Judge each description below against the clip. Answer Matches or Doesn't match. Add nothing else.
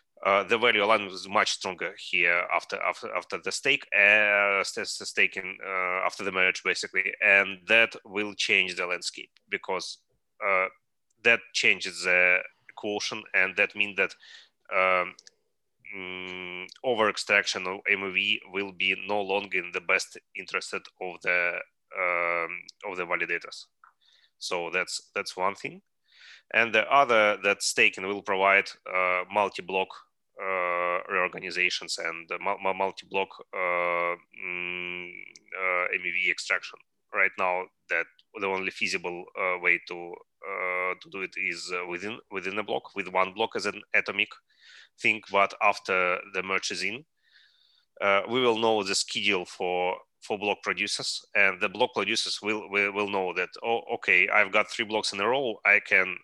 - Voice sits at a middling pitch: Doesn't match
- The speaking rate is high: Doesn't match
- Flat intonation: Matches